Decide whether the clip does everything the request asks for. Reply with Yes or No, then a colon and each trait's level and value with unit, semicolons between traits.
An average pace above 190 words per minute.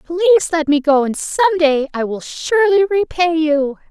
No: average, 185 wpm